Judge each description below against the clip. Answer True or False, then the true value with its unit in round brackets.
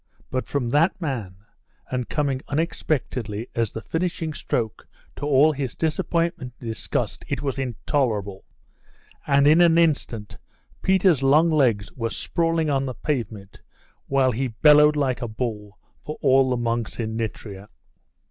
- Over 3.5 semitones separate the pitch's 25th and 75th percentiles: True (4.9 semitones)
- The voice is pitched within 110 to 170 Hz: True (135 Hz)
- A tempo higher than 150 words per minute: False (145 wpm)